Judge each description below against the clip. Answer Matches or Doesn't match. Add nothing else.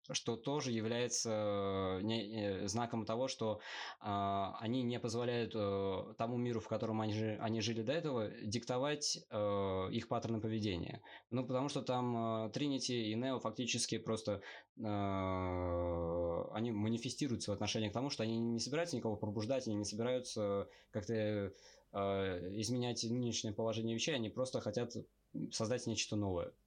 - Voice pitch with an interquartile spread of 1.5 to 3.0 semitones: Matches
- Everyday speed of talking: Matches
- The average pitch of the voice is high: Doesn't match